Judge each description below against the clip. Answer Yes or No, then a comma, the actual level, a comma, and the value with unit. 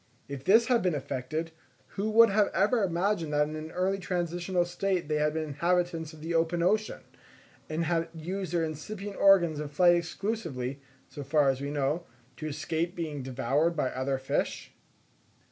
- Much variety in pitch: No, average, 3.6 semitones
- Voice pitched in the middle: Yes, medium, 165 Hz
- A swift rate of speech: No, average, 175 wpm